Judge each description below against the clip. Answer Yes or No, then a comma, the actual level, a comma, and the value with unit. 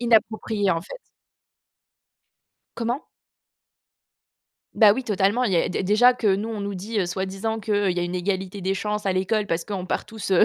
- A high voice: Yes, high, 200 Hz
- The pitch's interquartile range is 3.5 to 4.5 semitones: No, average, 2.7 semitones